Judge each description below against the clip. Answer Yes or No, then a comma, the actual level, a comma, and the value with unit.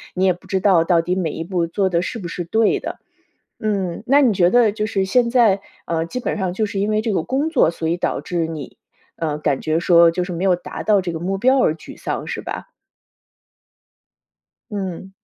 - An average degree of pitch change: Yes, average, 4.0 semitones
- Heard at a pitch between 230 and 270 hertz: No, medium, 185 Hz